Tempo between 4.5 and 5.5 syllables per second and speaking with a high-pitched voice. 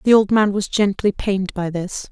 Yes: 5.1 syllables/s; high, 200 Hz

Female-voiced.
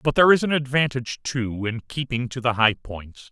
No: male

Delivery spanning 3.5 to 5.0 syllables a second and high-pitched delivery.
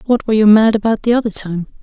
No: 6.8 syllables/s; high, 215 Hz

